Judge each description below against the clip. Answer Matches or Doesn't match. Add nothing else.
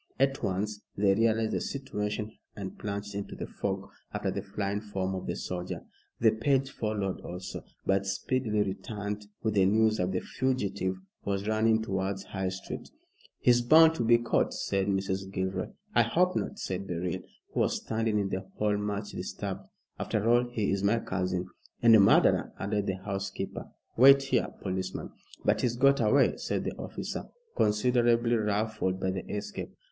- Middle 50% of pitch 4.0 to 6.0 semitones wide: Doesn't match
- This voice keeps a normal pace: Matches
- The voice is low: Matches